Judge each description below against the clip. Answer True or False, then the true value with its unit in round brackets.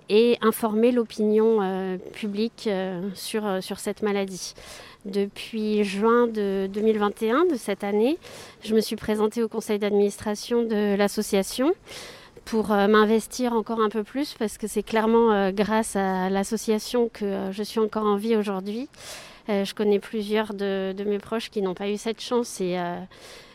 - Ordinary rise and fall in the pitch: False (1.9 semitones)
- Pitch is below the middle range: False (215 Hz)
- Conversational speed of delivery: True (170 wpm)